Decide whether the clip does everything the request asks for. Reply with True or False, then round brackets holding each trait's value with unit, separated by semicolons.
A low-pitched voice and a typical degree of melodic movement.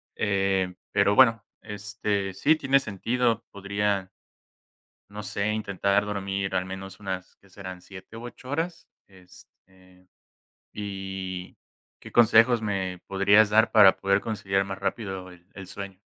False (100 Hz; 2.0 semitones)